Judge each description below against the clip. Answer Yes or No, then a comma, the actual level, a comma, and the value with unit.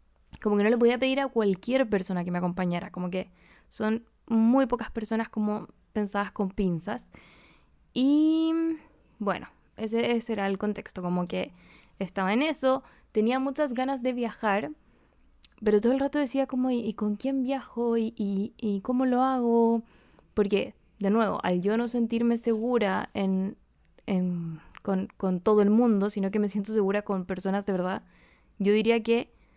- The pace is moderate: Yes, average, 170 wpm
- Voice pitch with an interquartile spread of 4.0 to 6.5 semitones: No, average, 3.5 semitones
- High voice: Yes, high, 215 Hz